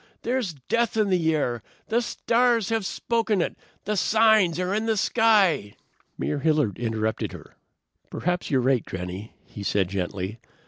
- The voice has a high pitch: No, medium, 180 Hz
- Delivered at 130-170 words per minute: Yes, average, 150 wpm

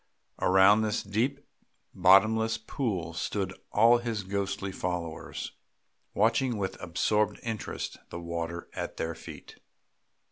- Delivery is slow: Yes, slow, 110 wpm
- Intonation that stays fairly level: No, average, 3.9 semitones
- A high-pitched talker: No, low, 100 Hz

